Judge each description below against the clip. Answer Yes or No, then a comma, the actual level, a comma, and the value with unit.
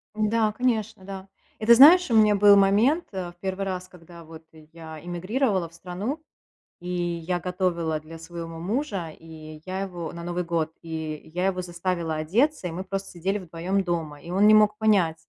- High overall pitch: No, medium, 180 Hz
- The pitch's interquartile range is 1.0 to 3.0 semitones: No, average, 3.5 semitones